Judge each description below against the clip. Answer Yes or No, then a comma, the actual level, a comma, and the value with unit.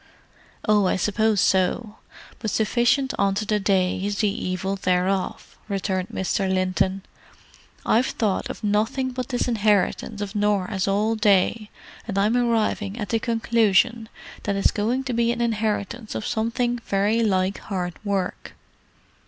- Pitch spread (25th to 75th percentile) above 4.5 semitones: No, average, 2.8 semitones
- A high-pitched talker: Yes, high, 210 Hz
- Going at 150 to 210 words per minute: No, average, 140 wpm